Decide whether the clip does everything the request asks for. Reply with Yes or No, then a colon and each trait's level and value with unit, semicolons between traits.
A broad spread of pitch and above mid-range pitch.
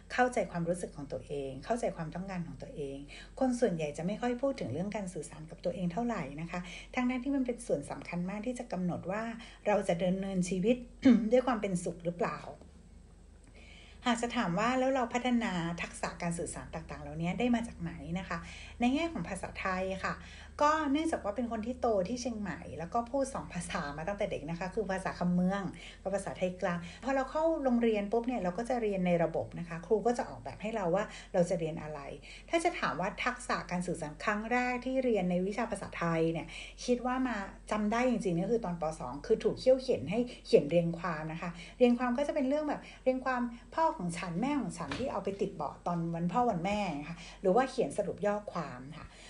Yes: wide, 6.0 semitones; high, 200 Hz